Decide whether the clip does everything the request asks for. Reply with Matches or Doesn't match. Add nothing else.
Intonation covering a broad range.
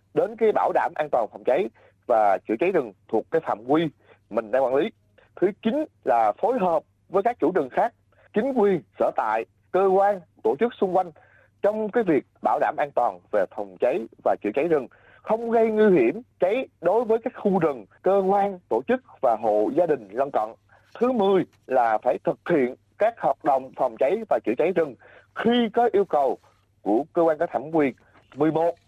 Matches